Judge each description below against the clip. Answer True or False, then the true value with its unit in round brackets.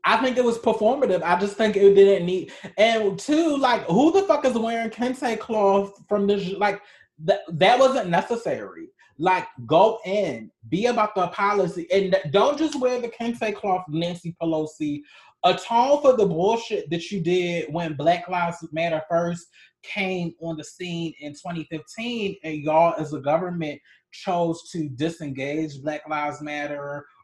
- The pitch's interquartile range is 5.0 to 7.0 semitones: True (5.4 semitones)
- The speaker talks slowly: False (160 wpm)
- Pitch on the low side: False (185 Hz)